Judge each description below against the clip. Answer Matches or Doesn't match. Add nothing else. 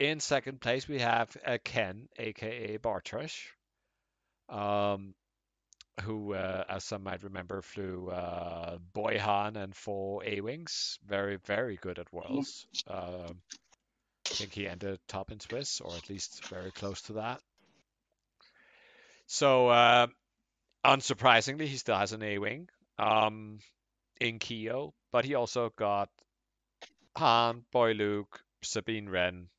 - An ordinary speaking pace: Doesn't match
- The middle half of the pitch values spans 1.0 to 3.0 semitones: Doesn't match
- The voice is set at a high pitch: Doesn't match